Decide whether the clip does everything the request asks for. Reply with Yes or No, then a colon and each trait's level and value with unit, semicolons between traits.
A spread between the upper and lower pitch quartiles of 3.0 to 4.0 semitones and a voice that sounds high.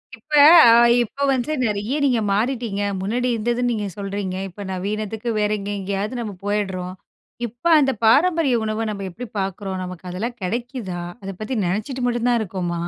Yes: average, 3.7 semitones; high, 215 Hz